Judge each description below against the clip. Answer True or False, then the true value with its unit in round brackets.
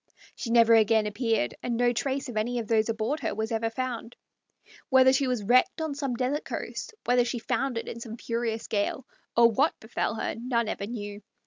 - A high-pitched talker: True (235 Hz)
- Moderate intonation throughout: False (2.2 semitones)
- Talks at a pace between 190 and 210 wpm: True (200 wpm)